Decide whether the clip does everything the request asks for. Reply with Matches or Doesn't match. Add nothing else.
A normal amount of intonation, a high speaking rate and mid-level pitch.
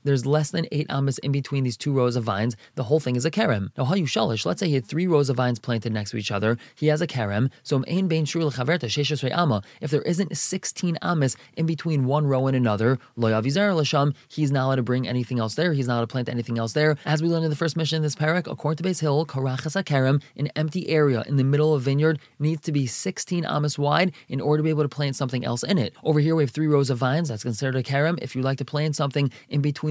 Matches